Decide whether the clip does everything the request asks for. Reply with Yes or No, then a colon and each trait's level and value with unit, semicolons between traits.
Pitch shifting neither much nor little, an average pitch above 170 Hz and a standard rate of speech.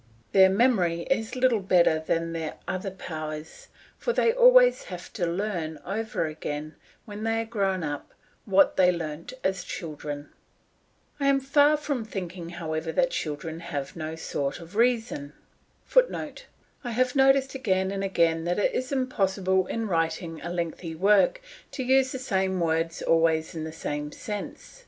No: wide, 6.2 semitones; medium, 185 Hz; average, 160 wpm